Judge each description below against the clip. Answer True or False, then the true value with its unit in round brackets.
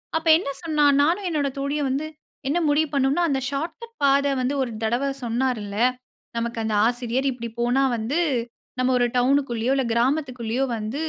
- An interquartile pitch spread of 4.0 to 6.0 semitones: False (3.2 semitones)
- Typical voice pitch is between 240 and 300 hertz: True (270 Hz)